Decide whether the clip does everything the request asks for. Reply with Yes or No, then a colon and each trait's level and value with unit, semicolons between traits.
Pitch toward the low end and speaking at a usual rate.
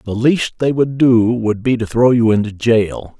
No: low, 115 Hz; fast, 225 wpm